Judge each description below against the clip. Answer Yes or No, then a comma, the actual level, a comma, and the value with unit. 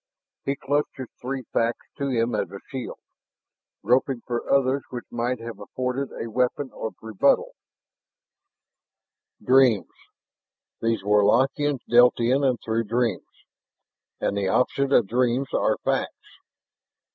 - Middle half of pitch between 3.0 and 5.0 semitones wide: No, narrow, 2.6 semitones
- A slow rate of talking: Yes, slow, 125 wpm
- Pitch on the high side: No, low, 125 Hz